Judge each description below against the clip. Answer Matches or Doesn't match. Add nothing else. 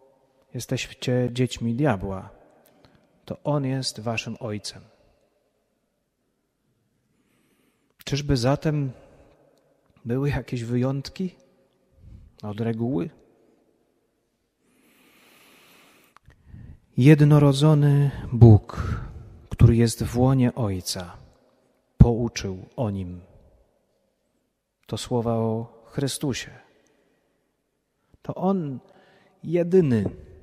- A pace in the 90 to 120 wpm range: Doesn't match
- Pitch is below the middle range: Matches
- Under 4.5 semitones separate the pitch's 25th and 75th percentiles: Matches